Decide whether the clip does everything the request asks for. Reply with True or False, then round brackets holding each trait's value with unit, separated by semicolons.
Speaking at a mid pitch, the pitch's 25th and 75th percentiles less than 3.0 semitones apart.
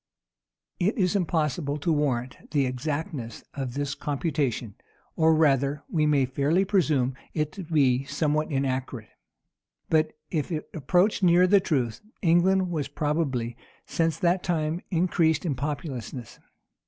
False (150 Hz; 3.7 semitones)